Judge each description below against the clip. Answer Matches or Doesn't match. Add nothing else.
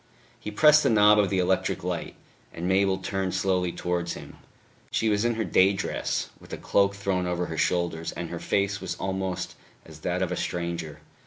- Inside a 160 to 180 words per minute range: Doesn't match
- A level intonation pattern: Matches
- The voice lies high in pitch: Doesn't match